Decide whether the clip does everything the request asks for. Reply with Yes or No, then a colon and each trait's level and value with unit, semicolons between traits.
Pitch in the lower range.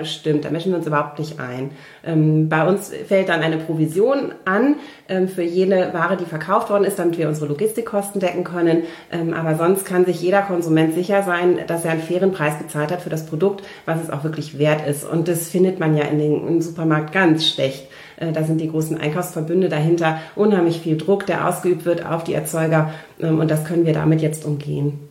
No: medium, 165 Hz